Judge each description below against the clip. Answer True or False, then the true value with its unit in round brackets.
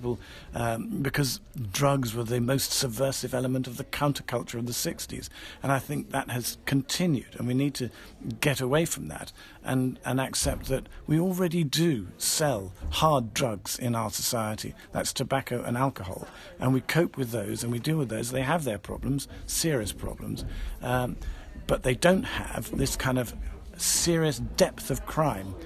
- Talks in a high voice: False (125 Hz)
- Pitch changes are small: False (3.1 semitones)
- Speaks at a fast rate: False (170 wpm)